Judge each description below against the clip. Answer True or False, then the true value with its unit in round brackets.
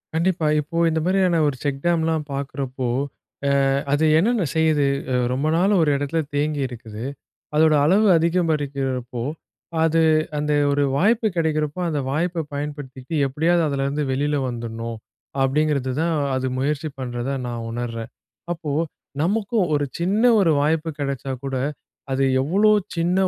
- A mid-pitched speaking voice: True (150 Hz)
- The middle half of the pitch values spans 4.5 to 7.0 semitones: False (3.6 semitones)